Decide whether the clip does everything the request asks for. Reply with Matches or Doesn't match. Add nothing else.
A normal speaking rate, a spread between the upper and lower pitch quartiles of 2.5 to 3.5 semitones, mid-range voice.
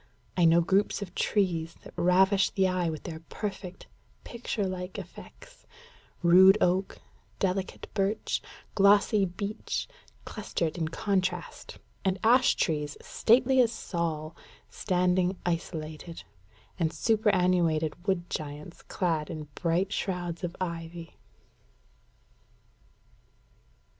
Doesn't match